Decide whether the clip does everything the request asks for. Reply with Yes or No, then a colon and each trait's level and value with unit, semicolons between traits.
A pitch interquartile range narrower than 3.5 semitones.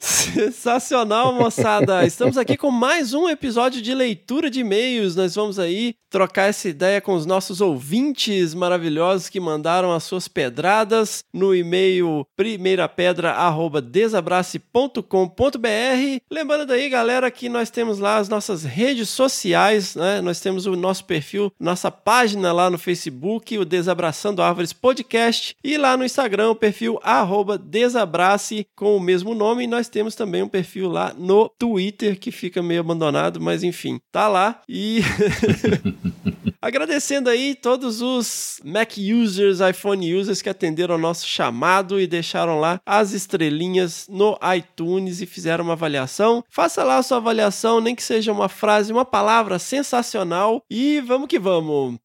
No: average, 4.6 semitones